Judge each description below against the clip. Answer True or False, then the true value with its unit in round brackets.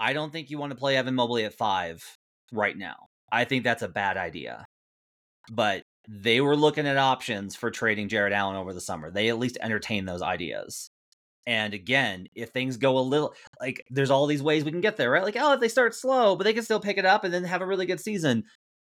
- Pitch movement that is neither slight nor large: False (7.3 semitones)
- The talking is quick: True (240 wpm)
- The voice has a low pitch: True (130 Hz)